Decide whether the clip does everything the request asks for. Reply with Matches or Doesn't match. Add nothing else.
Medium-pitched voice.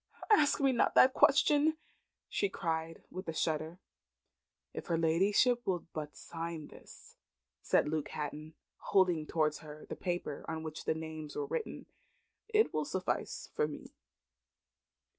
Matches